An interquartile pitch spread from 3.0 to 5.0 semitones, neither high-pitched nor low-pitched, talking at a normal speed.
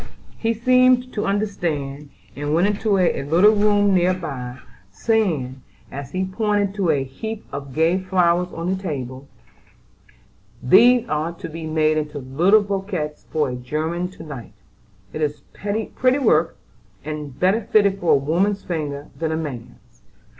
No: wide, 5.5 semitones; medium, 170 Hz; average, 155 wpm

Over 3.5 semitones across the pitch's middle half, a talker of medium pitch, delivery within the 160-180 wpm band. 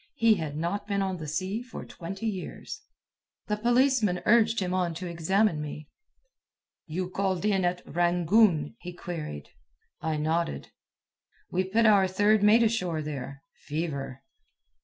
No: average, 4.5 semitones; medium, 180 Hz; average, 140 wpm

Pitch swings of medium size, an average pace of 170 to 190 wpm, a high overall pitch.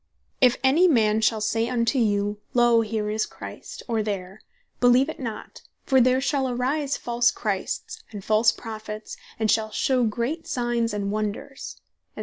No: average, 3.0 semitones; average, 160 wpm; high, 230 Hz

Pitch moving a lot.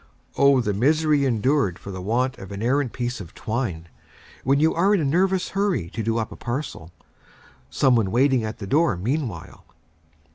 Yes: wide, 5.8 semitones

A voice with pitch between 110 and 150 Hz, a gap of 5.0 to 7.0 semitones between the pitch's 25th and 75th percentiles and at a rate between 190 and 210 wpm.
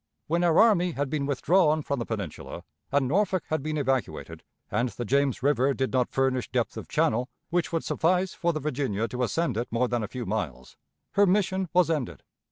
Yes: medium, 140 Hz; wide, 5.4 semitones; average, 200 wpm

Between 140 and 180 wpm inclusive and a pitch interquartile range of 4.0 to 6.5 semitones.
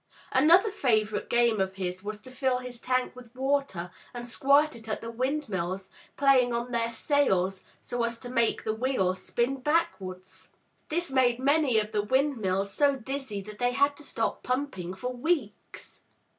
Yes: average, 170 wpm; average, 4.6 semitones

